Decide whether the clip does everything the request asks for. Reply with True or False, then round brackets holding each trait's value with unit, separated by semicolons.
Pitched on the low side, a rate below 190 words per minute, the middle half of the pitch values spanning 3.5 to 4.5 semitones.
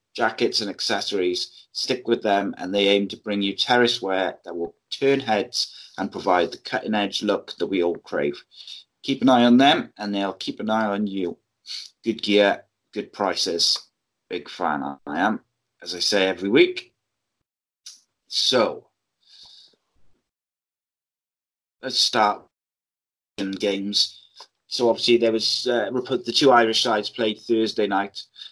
False (110 Hz; 145 wpm; 3.1 semitones)